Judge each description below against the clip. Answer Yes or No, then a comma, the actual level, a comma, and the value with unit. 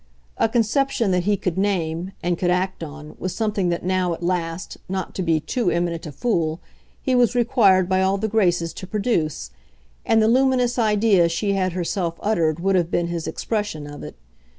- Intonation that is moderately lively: Yes, average, 4.1 semitones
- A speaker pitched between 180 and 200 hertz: Yes, medium, 185 Hz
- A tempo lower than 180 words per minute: No, average, 195 wpm